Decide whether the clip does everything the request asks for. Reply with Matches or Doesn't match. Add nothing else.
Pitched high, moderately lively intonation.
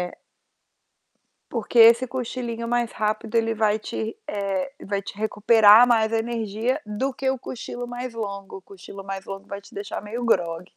Matches